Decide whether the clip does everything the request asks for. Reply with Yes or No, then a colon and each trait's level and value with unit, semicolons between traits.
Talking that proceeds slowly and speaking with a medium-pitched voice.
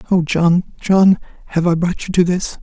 No: fast, 205 wpm; medium, 175 Hz